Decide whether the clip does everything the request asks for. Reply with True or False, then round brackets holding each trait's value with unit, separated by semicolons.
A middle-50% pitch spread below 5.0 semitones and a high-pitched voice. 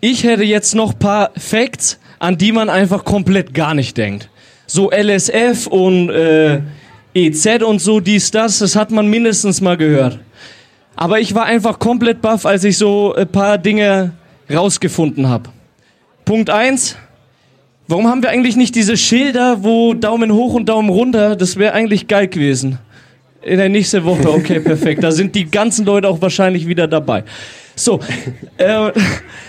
False (5.3 semitones; 200 Hz)